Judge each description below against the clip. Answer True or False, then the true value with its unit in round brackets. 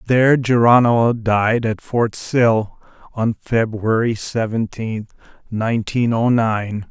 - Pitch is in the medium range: False (115 Hz)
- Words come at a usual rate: False (105 wpm)